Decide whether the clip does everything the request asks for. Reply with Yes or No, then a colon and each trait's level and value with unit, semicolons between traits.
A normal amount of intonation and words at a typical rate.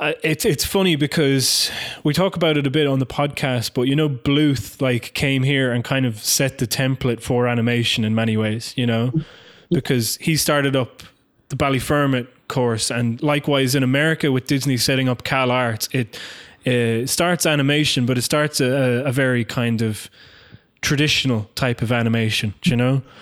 Yes: average, 3.3 semitones; average, 180 wpm